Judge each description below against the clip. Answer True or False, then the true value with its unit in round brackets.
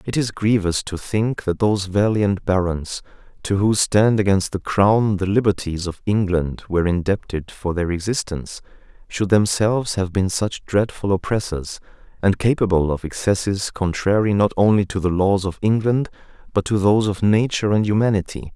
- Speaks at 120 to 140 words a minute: False (160 wpm)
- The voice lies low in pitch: True (100 Hz)